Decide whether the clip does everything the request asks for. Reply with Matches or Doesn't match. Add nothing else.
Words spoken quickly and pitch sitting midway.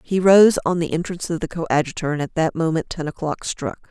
Matches